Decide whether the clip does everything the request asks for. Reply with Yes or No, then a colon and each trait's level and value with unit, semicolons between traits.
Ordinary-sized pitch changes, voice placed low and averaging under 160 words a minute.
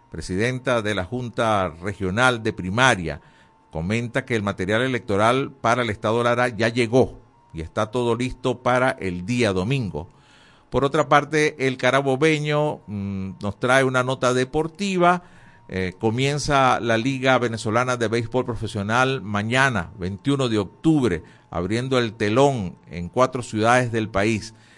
Yes: average, 3.8 semitones; low, 120 Hz; average, 140 wpm